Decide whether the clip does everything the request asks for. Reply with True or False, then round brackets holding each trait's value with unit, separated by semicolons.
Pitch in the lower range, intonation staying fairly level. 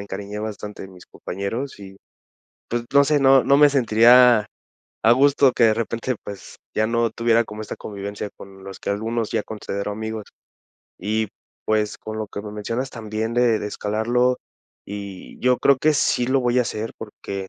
False (110 Hz; 3.0 semitones)